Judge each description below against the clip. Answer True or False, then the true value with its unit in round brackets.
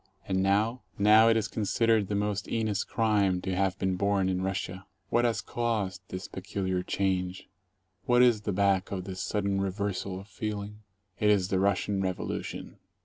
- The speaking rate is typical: True (165 wpm)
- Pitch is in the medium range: False (100 Hz)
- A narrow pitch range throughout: True (2.0 semitones)